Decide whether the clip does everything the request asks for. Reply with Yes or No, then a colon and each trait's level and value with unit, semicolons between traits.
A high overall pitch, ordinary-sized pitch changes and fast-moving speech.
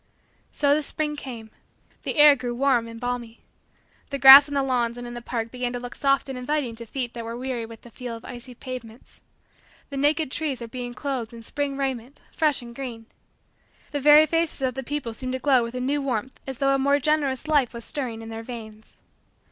Yes: very high, 255 Hz; average, 3.0 semitones; fast, 220 wpm